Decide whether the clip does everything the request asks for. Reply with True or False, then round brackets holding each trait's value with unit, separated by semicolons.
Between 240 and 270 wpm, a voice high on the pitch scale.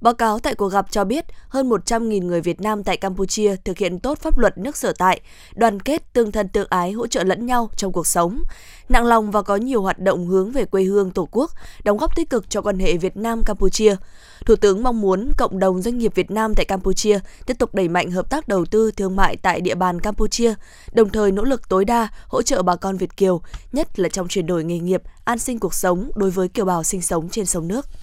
True (245 wpm; 205 Hz)